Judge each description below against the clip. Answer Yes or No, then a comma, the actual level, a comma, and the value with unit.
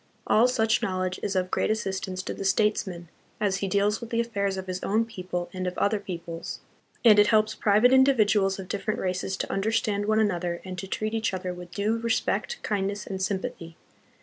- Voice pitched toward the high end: Yes, high, 200 Hz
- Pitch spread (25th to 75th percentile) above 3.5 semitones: No, average, 2.7 semitones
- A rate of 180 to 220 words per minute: Yes, average, 200 wpm